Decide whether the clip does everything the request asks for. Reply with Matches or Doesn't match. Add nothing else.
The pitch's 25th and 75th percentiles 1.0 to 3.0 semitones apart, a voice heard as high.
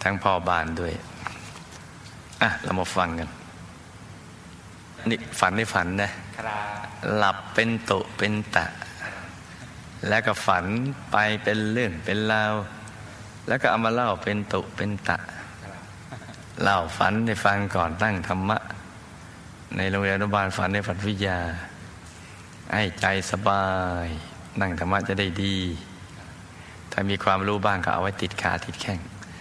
Doesn't match